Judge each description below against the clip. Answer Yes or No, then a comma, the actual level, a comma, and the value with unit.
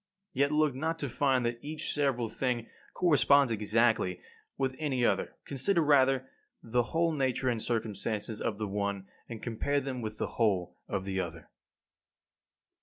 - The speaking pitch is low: Yes, low, 125 Hz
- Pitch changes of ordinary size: Yes, average, 4.5 semitones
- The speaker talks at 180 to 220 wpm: No, average, 155 wpm